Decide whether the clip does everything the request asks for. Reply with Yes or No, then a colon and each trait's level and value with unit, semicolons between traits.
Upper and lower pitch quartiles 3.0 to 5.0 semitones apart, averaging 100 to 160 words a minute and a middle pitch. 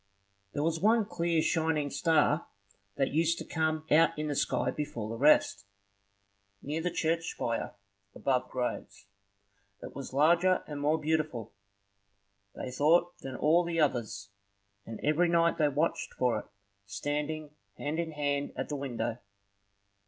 Yes: average, 3.5 semitones; average, 150 wpm; medium, 150 Hz